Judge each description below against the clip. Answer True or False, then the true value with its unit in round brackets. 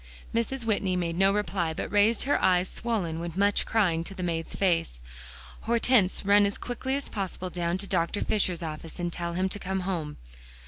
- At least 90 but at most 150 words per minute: False (190 wpm)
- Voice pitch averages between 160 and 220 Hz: True (190 Hz)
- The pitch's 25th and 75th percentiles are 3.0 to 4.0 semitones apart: True (3.3 semitones)